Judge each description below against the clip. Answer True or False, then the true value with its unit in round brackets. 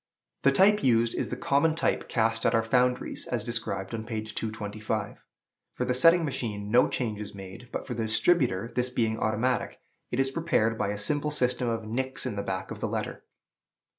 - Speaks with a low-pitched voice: True (115 Hz)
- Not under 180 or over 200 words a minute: True (195 wpm)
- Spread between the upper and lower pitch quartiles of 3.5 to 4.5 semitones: False (2.9 semitones)